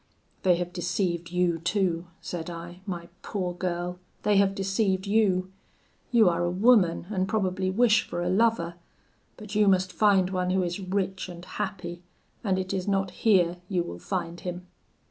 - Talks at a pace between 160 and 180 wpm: Yes, average, 170 wpm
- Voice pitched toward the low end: No, medium, 185 Hz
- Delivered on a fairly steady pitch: Yes, narrow, 2.0 semitones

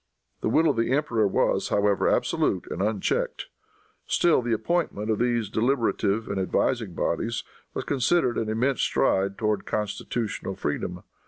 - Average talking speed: Yes, average, 145 wpm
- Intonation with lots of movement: No, average, 3.3 semitones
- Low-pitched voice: Yes, low, 110 Hz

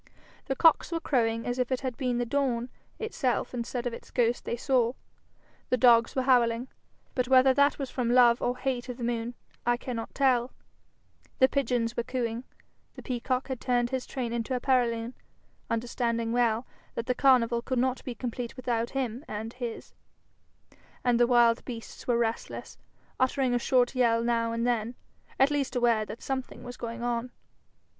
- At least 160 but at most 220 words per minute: Yes, average, 180 wpm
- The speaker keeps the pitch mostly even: Yes, narrow, 1.7 semitones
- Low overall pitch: No, high, 245 Hz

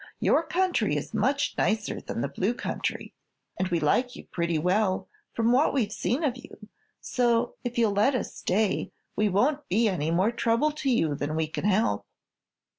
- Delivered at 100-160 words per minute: No, average, 185 wpm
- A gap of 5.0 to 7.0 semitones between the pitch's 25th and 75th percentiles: Yes, wide, 5.6 semitones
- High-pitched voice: Yes, high, 220 Hz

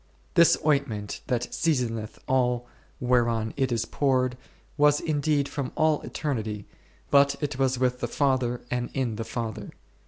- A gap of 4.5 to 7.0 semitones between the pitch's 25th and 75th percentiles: No, average, 3.0 semitones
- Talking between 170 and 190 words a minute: No, average, 145 wpm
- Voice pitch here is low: Yes, low, 125 Hz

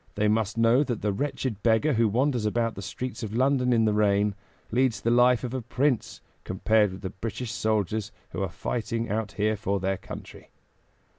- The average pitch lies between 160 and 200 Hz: No, low, 110 Hz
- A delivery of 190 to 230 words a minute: Yes, average, 195 wpm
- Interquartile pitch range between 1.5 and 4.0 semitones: Yes, average, 2.9 semitones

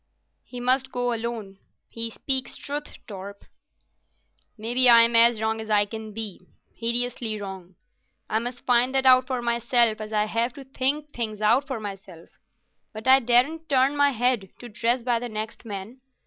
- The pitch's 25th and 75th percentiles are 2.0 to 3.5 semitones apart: Yes, average, 2.9 semitones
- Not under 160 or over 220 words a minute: Yes, average, 165 wpm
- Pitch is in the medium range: No, high, 235 Hz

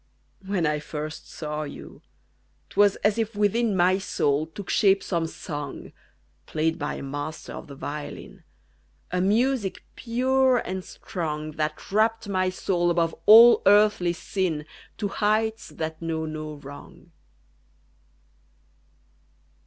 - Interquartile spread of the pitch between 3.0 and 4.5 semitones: No, average, 5.1 semitones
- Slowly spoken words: Yes, slow, 130 wpm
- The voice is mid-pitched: Yes, medium, 180 Hz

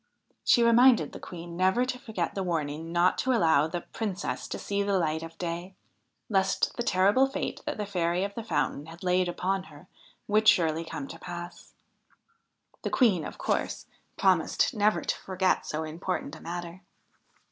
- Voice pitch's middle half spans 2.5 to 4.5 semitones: Yes, average, 3.5 semitones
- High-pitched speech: No, medium, 180 Hz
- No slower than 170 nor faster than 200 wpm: Yes, average, 175 wpm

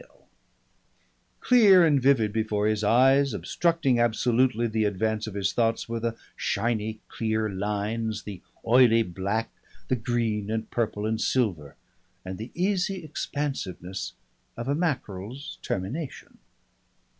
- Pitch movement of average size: Yes, average, 3.9 semitones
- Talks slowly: Yes, slow, 125 wpm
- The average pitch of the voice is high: No, low, 115 Hz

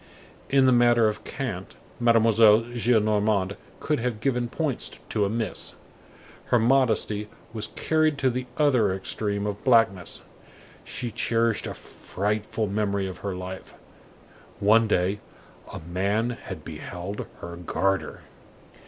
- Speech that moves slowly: Yes, slow, 125 wpm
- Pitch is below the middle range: Yes, low, 110 Hz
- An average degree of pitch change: Yes, average, 3.4 semitones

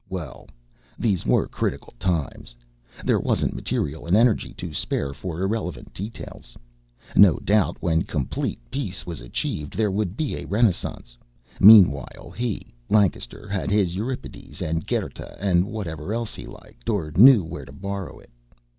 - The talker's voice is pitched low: Yes, very low, 95 Hz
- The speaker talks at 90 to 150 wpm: Yes, average, 145 wpm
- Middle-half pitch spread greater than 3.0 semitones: Yes, average, 4.8 semitones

